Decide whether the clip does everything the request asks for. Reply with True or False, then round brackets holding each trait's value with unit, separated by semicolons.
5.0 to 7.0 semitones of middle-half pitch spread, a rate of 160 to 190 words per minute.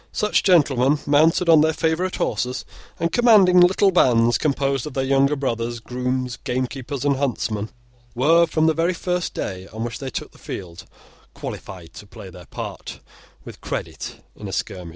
True (5.6 semitones; 170 wpm)